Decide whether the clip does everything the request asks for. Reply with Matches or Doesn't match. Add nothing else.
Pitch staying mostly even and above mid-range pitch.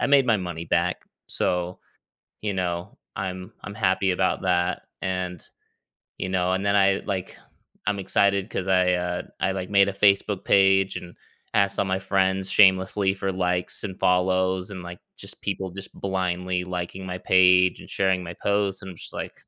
Doesn't match